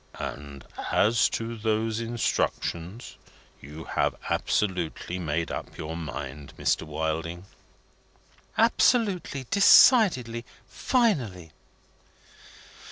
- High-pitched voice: No, low, 105 Hz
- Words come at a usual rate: No, slow, 80 wpm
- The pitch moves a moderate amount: No, wide, 7.0 semitones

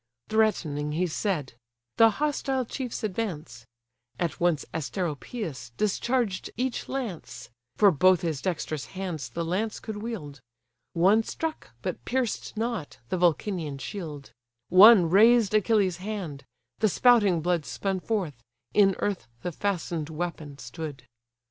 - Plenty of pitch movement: Yes, wide, 5.7 semitones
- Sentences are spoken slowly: Yes, slow, 125 wpm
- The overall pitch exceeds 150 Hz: Yes, medium, 185 Hz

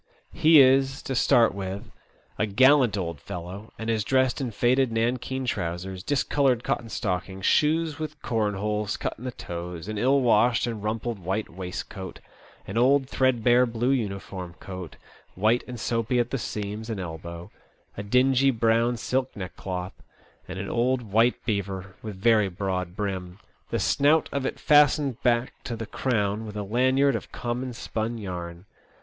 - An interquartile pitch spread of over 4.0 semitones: Yes, average, 4.7 semitones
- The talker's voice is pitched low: Yes, low, 115 Hz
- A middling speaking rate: Yes, average, 160 wpm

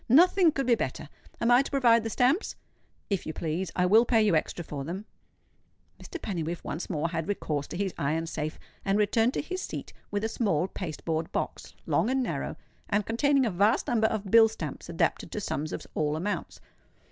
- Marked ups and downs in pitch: Yes, wide, 6.2 semitones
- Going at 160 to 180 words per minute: No, fast, 205 wpm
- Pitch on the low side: No, high, 205 Hz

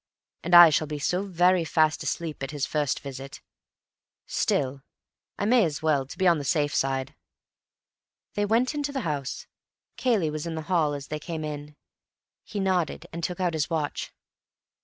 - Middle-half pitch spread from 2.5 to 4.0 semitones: Yes, average, 3.6 semitones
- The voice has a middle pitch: Yes, medium, 160 Hz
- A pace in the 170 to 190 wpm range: Yes, average, 175 wpm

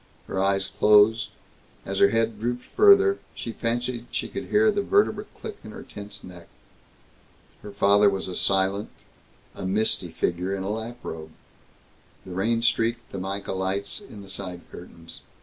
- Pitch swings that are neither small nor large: Yes, average, 3.5 semitones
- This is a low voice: Yes, low, 100 Hz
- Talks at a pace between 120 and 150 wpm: No, average, 160 wpm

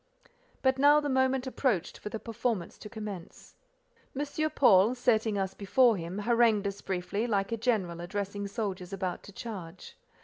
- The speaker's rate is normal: Yes, average, 160 wpm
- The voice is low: No, high, 210 Hz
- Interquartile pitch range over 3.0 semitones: Yes, average, 3.9 semitones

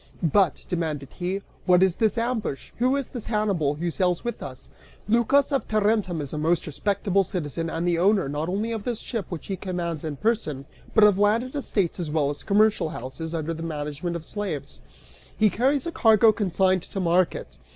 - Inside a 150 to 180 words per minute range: No, average, 195 wpm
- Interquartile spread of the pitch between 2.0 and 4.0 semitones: No, average, 4.9 semitones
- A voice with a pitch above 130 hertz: Yes, medium, 185 Hz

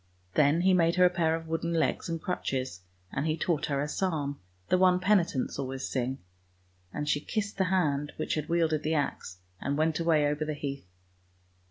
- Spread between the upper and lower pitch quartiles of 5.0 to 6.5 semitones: No, average, 3.1 semitones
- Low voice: No, medium, 155 Hz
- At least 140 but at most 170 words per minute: No, average, 195 wpm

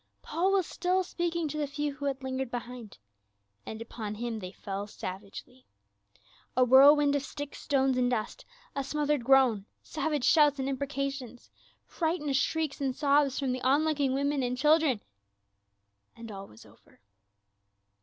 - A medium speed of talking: Yes, average, 155 wpm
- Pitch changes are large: No, average, 3.2 semitones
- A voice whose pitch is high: Yes, very high, 275 Hz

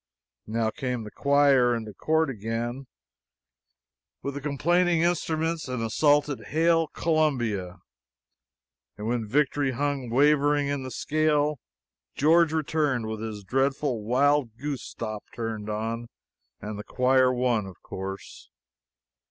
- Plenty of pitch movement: No, average, 4.6 semitones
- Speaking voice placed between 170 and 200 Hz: No, low, 130 Hz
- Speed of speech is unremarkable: No, slow, 120 wpm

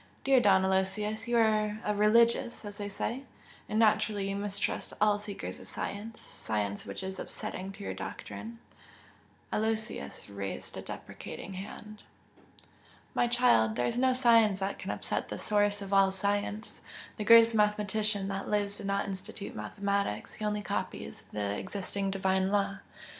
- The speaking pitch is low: No, high, 205 Hz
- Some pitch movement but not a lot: No, narrow, 1.9 semitones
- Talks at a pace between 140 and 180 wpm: Yes, average, 155 wpm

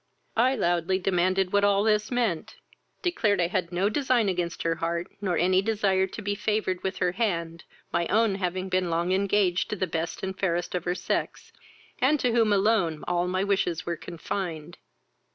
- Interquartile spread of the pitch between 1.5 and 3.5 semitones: Yes, average, 2.9 semitones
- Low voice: No, medium, 185 Hz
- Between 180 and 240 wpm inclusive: Yes, average, 185 wpm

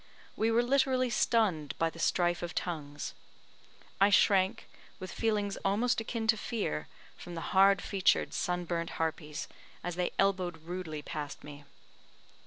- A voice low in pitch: No, medium, 185 Hz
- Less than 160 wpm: Yes, average, 145 wpm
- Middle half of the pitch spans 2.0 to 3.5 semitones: No, average, 4.8 semitones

